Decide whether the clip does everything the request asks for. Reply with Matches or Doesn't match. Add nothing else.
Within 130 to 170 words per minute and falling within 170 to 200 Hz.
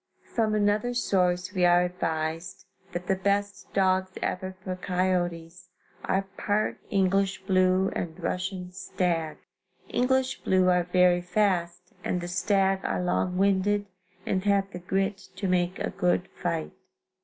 Matches